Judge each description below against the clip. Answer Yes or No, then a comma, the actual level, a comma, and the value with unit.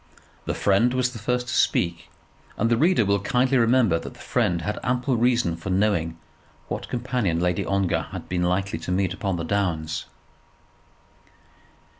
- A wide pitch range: Yes, wide, 5.7 semitones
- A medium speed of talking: Yes, average, 165 wpm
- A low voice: Yes, low, 100 Hz